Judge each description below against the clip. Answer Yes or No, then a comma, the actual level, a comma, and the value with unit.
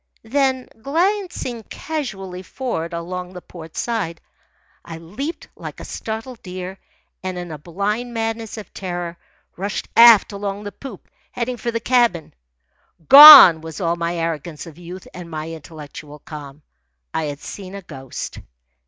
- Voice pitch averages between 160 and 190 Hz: Yes, medium, 185 Hz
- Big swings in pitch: Yes, wide, 5.7 semitones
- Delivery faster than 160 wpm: No, average, 145 wpm